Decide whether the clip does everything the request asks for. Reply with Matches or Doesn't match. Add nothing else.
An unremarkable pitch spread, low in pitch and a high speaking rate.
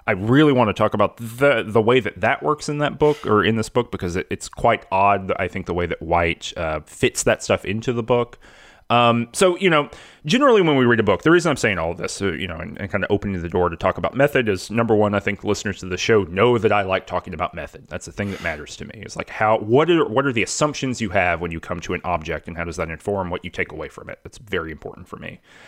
Matches